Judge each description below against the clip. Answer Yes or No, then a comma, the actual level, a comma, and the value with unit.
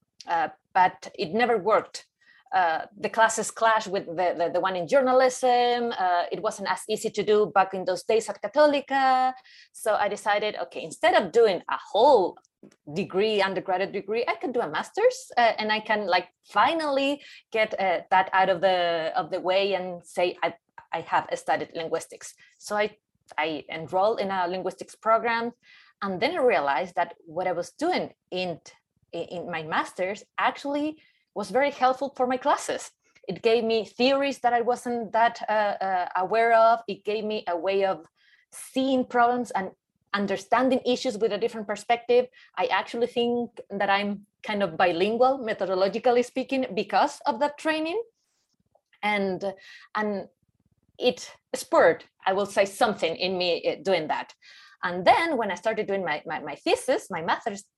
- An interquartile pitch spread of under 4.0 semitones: No, average, 4.7 semitones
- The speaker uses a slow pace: No, average, 165 wpm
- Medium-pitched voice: No, high, 215 Hz